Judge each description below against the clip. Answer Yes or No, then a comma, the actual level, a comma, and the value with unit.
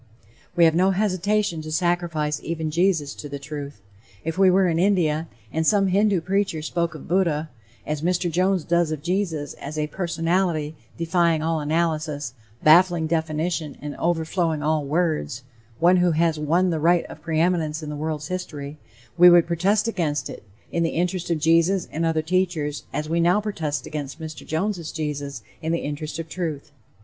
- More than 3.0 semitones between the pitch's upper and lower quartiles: No, narrow, 2.6 semitones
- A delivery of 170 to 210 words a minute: Yes, average, 175 wpm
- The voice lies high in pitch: No, medium, 165 Hz